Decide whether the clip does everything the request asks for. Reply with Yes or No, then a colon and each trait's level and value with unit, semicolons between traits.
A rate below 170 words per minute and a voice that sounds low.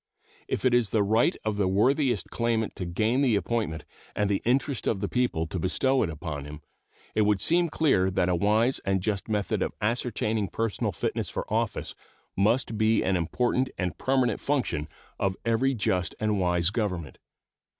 No: average, 180 wpm; low, 105 Hz